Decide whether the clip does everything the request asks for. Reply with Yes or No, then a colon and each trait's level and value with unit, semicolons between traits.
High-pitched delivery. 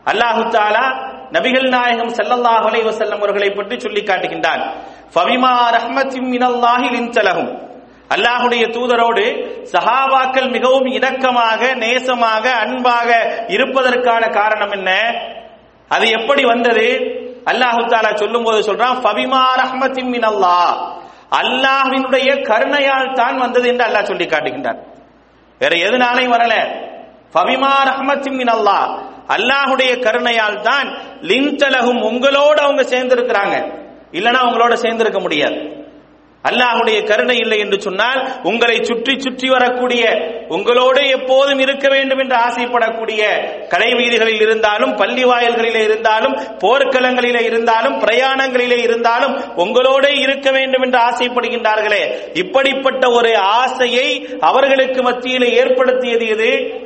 Yes: high, 245 Hz